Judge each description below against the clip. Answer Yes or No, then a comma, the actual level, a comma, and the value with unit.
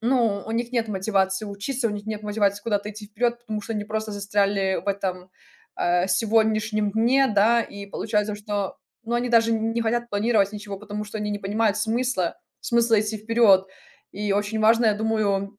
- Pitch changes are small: Yes, narrow, 2.0 semitones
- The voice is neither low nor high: No, high, 210 Hz